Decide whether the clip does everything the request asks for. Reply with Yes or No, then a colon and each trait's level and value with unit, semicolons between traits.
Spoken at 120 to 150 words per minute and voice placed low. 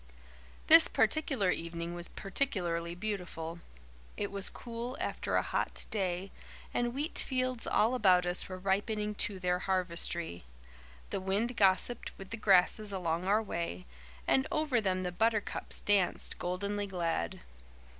No: slow, 135 wpm; high, 195 Hz